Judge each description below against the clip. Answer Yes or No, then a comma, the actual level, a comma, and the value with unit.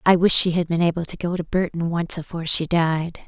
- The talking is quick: Yes, fast, 255 wpm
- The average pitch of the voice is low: No, medium, 170 Hz